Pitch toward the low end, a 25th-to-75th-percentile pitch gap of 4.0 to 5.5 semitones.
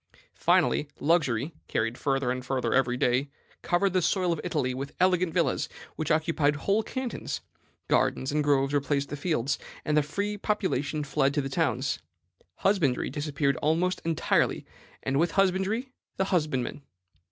No: medium, 150 Hz; average, 4.8 semitones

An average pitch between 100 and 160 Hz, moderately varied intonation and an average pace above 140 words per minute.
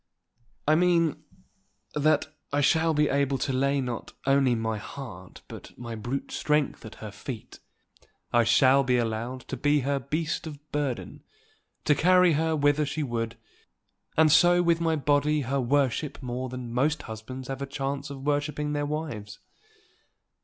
Yes: medium, 140 Hz; average, 3.3 semitones; average, 160 wpm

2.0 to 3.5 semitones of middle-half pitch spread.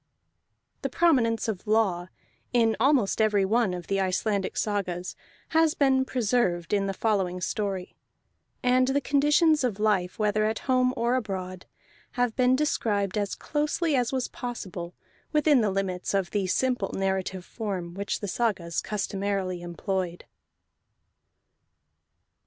No: average, 4.8 semitones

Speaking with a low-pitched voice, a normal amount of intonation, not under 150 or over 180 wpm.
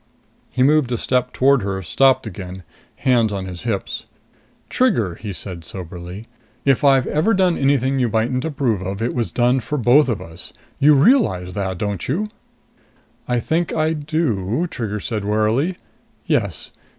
No: low, 120 Hz; wide, 5.9 semitones; average, 160 wpm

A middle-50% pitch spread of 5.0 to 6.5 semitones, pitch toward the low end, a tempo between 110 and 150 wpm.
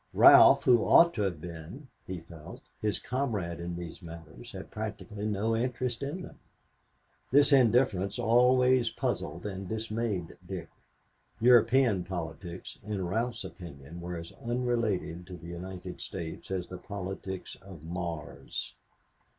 Yes: average, 5.3 semitones; very low, 95 Hz; slow, 135 wpm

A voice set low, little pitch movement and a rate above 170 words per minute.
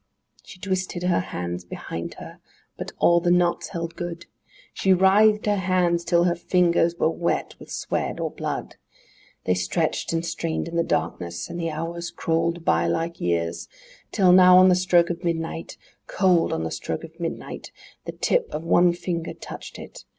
No: medium, 170 Hz; narrow, 1.6 semitones; average, 180 wpm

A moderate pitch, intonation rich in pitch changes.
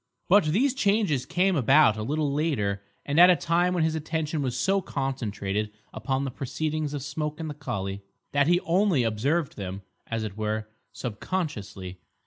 Yes: medium, 145 Hz; wide, 7.1 semitones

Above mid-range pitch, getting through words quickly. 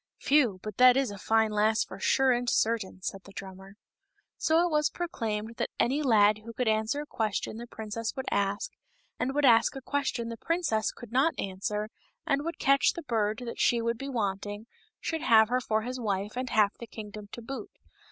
Yes: high, 230 Hz; fast, 210 wpm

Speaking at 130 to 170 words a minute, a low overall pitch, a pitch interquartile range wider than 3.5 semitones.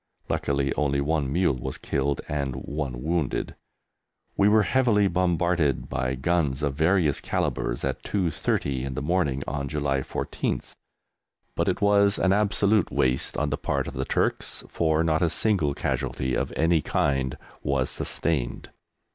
Yes: average, 150 wpm; very low, 75 Hz; average, 4.4 semitones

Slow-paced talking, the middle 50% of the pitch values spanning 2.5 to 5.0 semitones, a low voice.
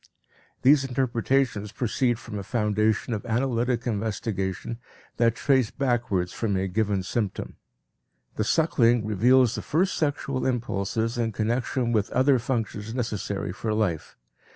Yes: slow, 130 wpm; average, 3.2 semitones; low, 115 Hz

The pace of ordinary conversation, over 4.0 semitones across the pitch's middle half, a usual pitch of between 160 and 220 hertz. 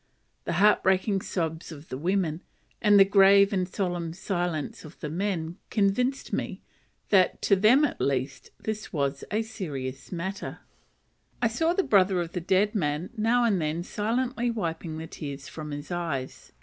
Yes: average, 160 wpm; average, 4.5 semitones; medium, 185 Hz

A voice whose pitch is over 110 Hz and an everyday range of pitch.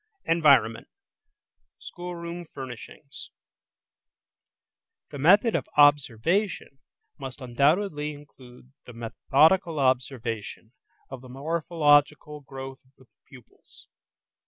Yes: medium, 140 Hz; average, 3.9 semitones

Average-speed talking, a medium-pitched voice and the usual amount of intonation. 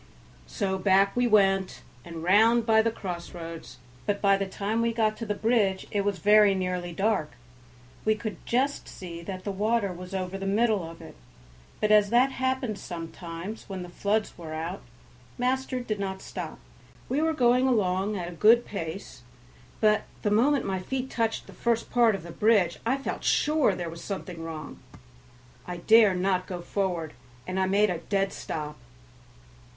No: average, 175 wpm; high, 200 Hz; average, 3.7 semitones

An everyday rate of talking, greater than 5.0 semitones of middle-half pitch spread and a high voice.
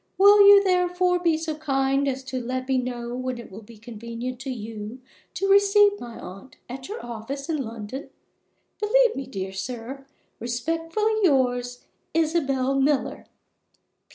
Yes: average, 150 wpm; wide, 5.5 semitones; very high, 265 Hz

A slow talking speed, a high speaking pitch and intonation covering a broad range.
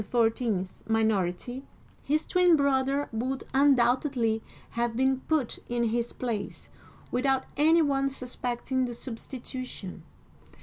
No: slow, 105 wpm; very high, 250 Hz; average, 3.0 semitones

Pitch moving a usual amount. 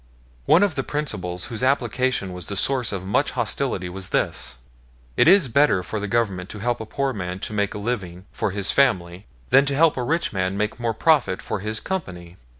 No: wide, 6.3 semitones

